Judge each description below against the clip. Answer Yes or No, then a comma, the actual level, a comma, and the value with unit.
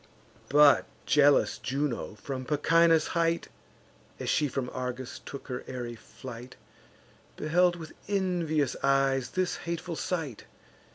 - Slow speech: Yes, slow, 115 wpm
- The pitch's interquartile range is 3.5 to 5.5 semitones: Yes, average, 4.4 semitones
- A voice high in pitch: No, medium, 145 Hz